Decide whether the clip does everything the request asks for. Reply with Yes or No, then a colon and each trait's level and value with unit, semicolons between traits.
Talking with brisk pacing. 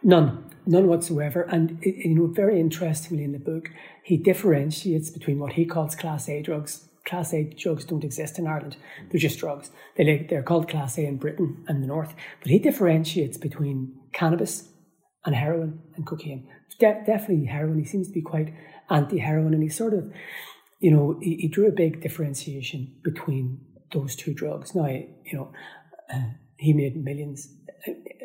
No: average, 170 wpm